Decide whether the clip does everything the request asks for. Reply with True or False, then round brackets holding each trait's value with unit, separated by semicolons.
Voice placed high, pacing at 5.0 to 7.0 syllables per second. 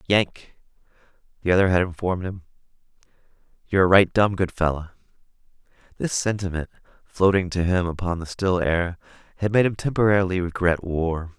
False (90 Hz; 5.5 syllables/s)